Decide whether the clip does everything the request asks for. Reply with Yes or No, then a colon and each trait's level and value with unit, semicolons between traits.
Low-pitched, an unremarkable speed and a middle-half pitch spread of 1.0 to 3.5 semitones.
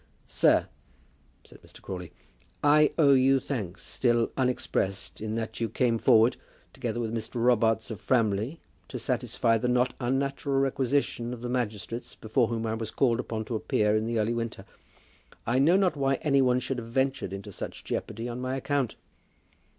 Yes: low, 120 Hz; average, 175 wpm; average, 3.0 semitones